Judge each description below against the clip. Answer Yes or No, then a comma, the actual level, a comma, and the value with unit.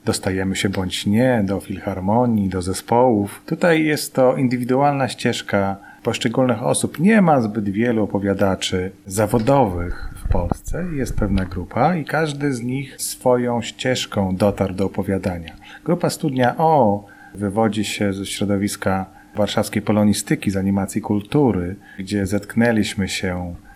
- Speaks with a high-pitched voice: No, low, 105 Hz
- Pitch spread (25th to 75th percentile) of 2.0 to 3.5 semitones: No, average, 4.2 semitones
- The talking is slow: No, average, 125 wpm